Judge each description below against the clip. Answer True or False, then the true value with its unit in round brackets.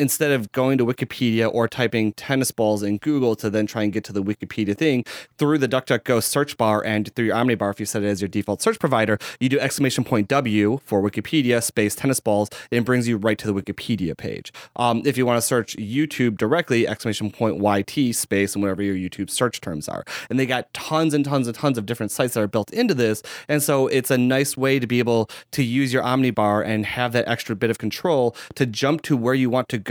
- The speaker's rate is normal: False (240 wpm)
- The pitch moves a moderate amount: True (3.7 semitones)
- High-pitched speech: False (120 Hz)